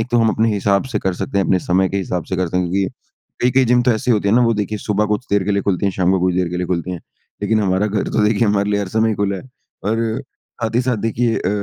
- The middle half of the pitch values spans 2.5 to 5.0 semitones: Yes, average, 2.9 semitones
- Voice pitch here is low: Yes, low, 100 Hz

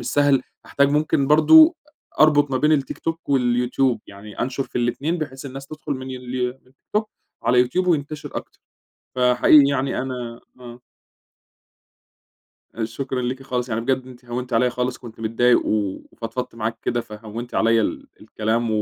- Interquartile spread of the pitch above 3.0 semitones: No, average, 2.7 semitones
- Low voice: Yes, low, 125 Hz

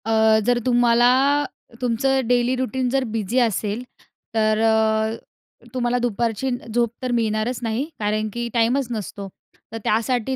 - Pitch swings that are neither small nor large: No, narrow, 2.1 semitones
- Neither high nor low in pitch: No, high, 235 Hz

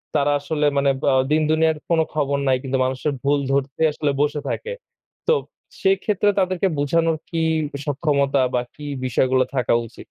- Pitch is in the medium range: Yes, medium, 145 Hz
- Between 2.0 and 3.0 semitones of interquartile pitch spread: Yes, average, 2.7 semitones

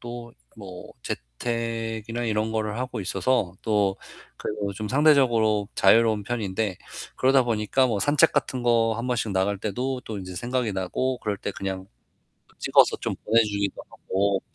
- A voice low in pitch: Yes, low, 110 Hz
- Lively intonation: No, average, 3.2 semitones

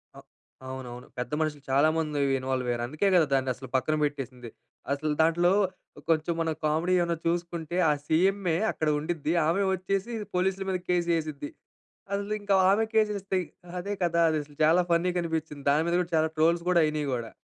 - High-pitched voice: No, medium, 160 Hz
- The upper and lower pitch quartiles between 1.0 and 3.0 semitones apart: No, average, 3.5 semitones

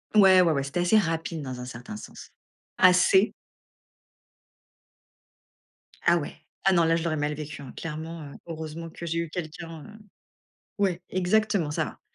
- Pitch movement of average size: Yes, average, 3.1 semitones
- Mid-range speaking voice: Yes, medium, 165 Hz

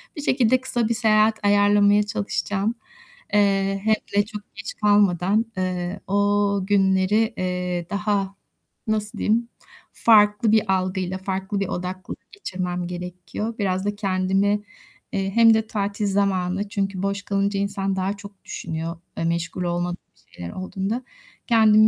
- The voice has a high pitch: Yes, high, 200 Hz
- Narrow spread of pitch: Yes, narrow, 2.0 semitones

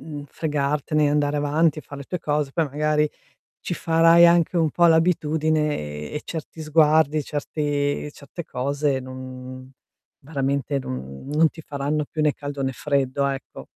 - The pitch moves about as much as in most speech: No, narrow, 2.1 semitones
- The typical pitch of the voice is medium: Yes, medium, 150 Hz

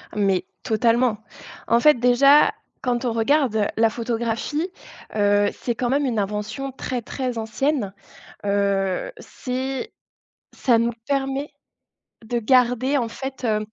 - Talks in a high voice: Yes, high, 240 Hz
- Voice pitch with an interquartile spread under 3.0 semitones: No, average, 3.5 semitones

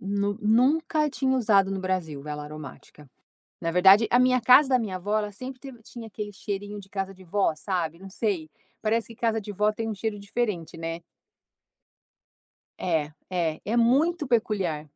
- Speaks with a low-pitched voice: No, high, 205 Hz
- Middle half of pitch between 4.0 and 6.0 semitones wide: Yes, average, 4.4 semitones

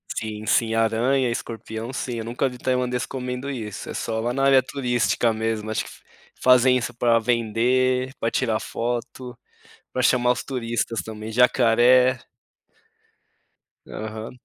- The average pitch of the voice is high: No, low, 120 Hz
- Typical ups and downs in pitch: No, narrow, 2.1 semitones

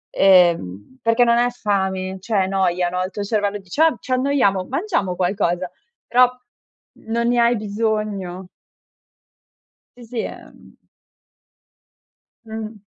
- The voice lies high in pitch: Yes, high, 205 Hz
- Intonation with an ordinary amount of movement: Yes, average, 4.0 semitones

